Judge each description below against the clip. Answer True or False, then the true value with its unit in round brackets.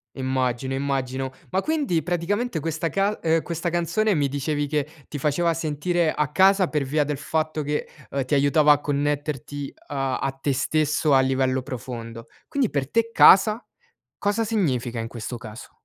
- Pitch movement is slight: False (4.2 semitones)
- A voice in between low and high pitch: True (150 Hz)